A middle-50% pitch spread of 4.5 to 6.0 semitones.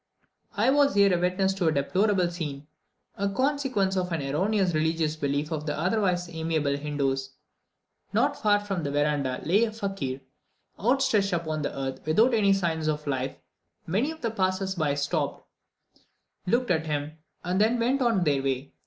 Yes: wide, 5.5 semitones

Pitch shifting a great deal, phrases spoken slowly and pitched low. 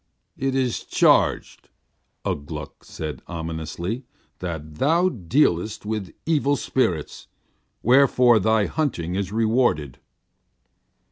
Yes: wide, 7.9 semitones; slow, 95 wpm; low, 105 Hz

